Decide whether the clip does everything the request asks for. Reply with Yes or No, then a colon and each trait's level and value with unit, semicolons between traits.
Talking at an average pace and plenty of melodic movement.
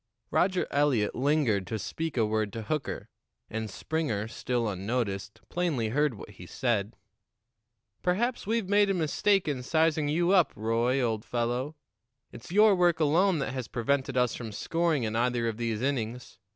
Yes: average, 165 wpm; wide, 6.3 semitones